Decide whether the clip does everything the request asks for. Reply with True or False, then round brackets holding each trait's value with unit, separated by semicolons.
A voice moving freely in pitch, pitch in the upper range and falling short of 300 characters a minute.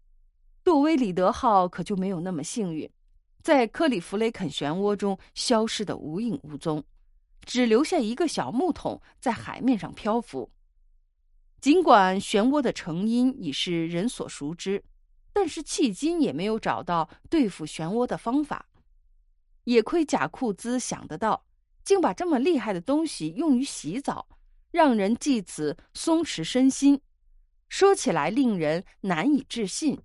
True (8.5 semitones; 220 Hz; 220 characters per minute)